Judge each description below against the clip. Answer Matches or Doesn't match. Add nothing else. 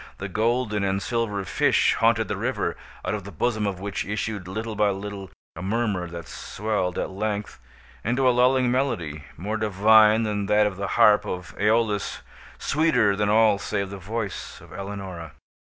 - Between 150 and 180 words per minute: Matches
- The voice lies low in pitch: Matches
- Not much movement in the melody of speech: Matches